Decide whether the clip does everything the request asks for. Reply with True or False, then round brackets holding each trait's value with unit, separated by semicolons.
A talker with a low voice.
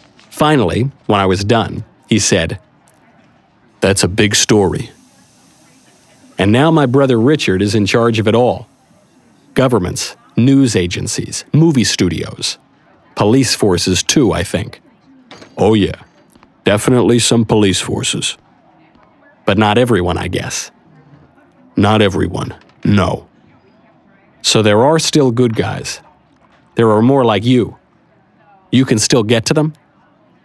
True (120 Hz)